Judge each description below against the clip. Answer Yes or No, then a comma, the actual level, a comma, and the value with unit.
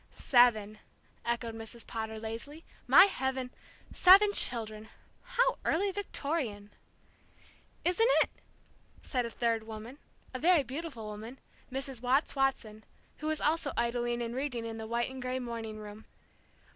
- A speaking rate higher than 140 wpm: No, slow, 135 wpm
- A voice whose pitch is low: No, high, 245 Hz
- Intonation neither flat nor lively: Yes, average, 4.3 semitones